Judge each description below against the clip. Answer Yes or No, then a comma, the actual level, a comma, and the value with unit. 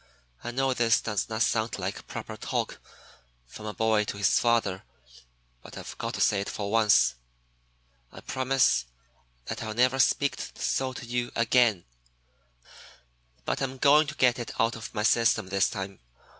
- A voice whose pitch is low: Yes, low, 115 Hz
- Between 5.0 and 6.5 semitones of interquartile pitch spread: No, average, 3.2 semitones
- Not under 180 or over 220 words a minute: No, average, 165 wpm